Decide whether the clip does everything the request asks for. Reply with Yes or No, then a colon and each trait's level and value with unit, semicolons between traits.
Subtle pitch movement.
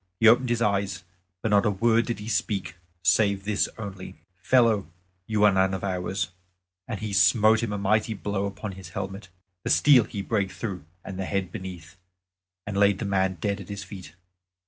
Yes: narrow, 2.2 semitones